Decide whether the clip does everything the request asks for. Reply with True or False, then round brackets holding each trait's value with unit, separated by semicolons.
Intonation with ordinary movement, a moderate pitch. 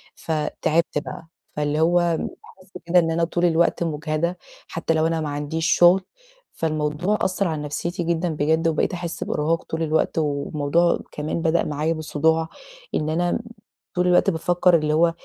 False (2.1 semitones; 160 Hz)